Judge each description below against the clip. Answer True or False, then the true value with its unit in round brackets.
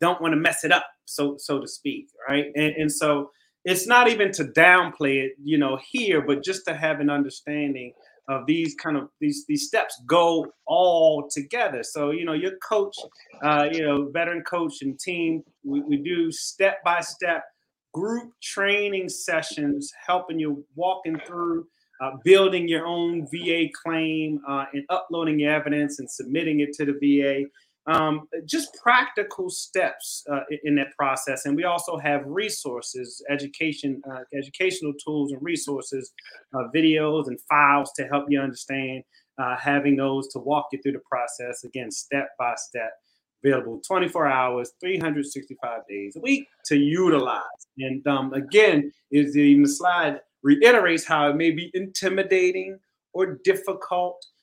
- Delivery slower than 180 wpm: True (160 wpm)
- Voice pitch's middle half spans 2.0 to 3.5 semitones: False (4.4 semitones)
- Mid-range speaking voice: True (155 Hz)